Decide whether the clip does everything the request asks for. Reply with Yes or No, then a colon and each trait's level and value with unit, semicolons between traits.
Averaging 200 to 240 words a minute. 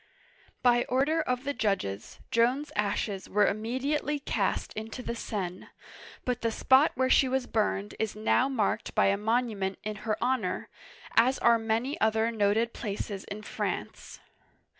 No: average, 155 wpm